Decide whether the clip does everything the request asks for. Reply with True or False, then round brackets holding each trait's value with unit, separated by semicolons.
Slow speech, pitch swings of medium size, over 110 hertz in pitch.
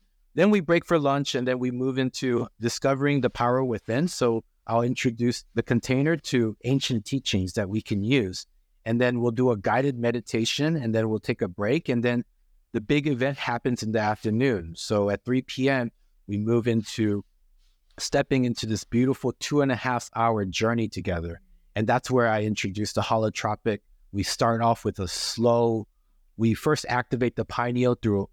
False (180 wpm; 3.2 semitones; 120 Hz)